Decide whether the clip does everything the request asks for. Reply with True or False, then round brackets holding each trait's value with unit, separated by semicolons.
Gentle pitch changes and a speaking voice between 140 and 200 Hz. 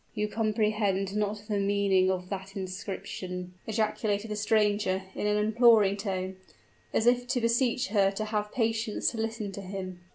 False (2.2 semitones; 210 Hz)